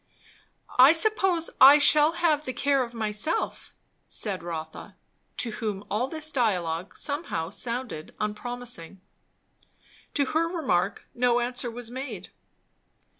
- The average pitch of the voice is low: No, high, 245 Hz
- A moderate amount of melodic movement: No, wide, 6.0 semitones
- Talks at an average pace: No, slow, 120 wpm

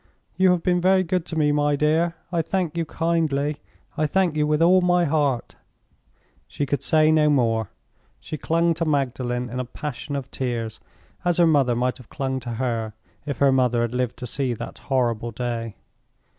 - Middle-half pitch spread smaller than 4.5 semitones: No, average, 4.8 semitones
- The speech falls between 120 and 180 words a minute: No, average, 190 wpm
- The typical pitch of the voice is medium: Yes, medium, 145 Hz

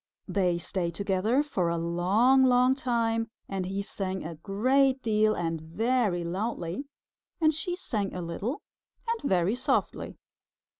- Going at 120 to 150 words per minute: Yes, average, 140 wpm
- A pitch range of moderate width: No, wide, 6.0 semitones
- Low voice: No, high, 205 Hz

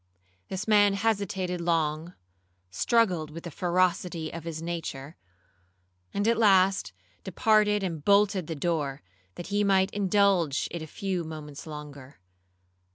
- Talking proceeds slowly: Yes, slow, 130 wpm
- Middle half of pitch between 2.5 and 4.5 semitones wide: Yes, average, 4.0 semitones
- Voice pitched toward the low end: No, medium, 175 Hz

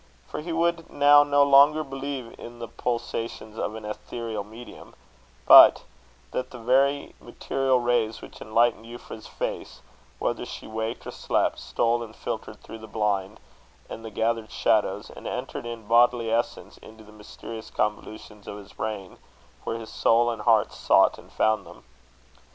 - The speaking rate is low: No, average, 160 wpm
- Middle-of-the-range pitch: No, low, 115 Hz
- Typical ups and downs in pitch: No, narrow, 2.3 semitones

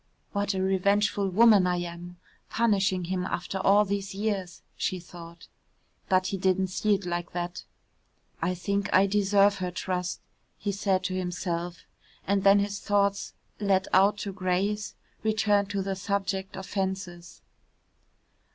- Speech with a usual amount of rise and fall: No, narrow, 1.8 semitones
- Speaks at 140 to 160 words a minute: Yes, average, 145 wpm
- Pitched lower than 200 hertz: Yes, high, 190 Hz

